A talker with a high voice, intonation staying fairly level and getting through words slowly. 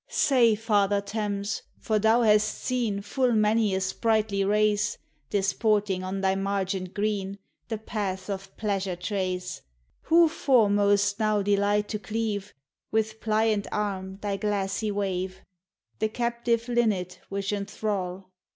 Yes: high, 205 Hz; narrow, 1.9 semitones; slow, 125 wpm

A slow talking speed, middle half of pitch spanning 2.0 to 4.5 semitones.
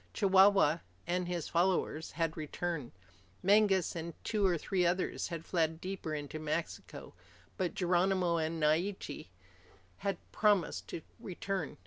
Yes: slow, 125 wpm; average, 2.9 semitones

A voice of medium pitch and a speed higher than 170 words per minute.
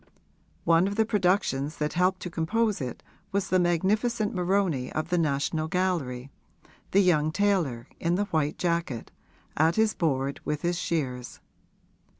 No: medium, 170 Hz; average, 150 wpm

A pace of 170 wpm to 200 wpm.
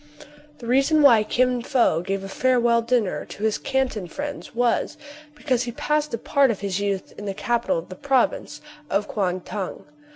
Yes: average, 185 wpm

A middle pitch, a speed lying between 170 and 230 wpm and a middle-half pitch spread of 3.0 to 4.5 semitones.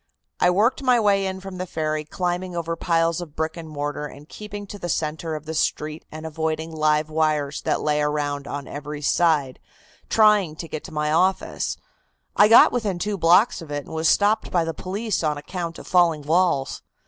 Yes: medium, 165 Hz; average, 200 wpm; average, 3.4 semitones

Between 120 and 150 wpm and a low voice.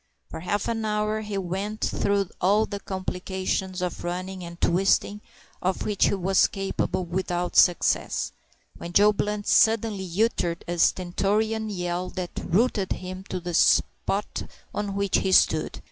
No: average, 145 wpm; high, 190 Hz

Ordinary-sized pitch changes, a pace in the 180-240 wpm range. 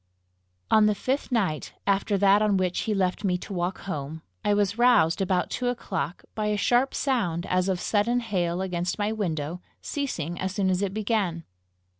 Yes: average, 3.2 semitones; average, 185 wpm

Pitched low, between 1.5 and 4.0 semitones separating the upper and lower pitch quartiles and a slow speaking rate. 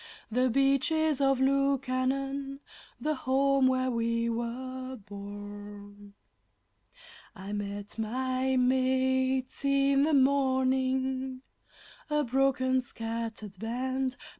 No: very high, 260 Hz; average, 2.7 semitones; slow, 90 wpm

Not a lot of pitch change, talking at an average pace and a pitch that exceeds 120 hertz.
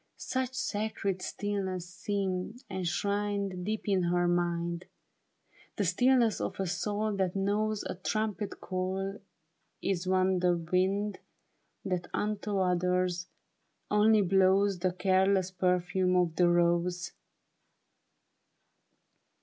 No: narrow, 2.2 semitones; slow, 105 wpm; high, 190 Hz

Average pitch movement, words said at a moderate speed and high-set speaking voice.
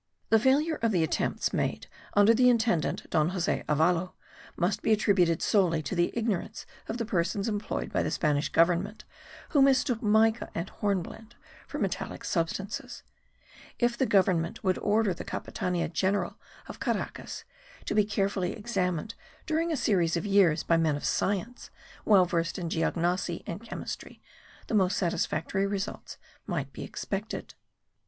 Yes: average, 4.4 semitones; average, 150 wpm; high, 195 Hz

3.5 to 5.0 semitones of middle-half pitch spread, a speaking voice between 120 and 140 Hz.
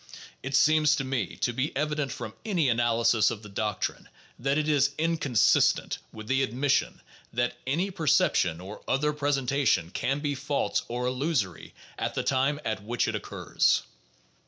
Yes: average, 3.9 semitones; low, 135 Hz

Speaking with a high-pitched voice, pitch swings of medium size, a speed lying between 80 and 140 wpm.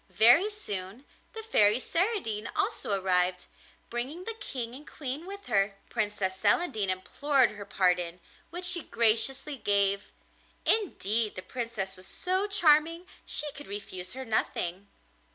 No: high, 235 Hz; wide, 8.9 semitones; slow, 135 wpm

